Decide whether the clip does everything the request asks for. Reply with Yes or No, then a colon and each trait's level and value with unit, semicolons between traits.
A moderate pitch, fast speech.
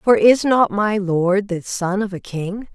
No: high, 200 Hz; fast, 220 wpm